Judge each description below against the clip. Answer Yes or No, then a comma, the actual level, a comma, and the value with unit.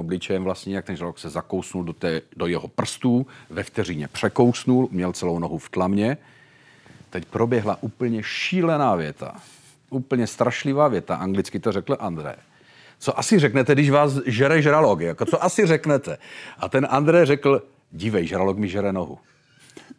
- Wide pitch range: Yes, wide, 7.1 semitones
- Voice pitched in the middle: No, low, 120 Hz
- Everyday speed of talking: Yes, average, 155 wpm